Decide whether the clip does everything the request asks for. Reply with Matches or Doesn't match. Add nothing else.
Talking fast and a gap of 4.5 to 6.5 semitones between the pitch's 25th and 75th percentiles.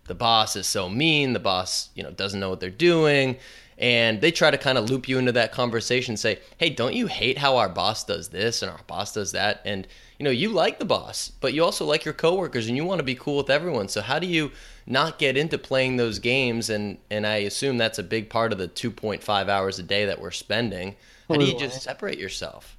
Matches